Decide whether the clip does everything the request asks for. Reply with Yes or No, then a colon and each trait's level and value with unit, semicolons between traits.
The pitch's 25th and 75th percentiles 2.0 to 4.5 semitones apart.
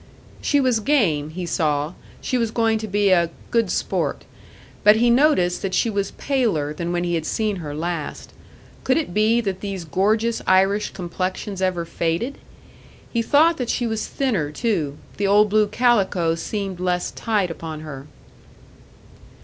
No: average, 4.9 semitones